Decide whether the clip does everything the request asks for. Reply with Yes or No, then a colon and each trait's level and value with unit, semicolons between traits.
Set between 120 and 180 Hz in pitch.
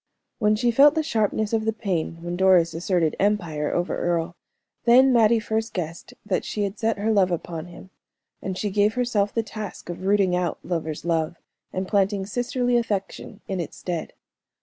No: high, 195 Hz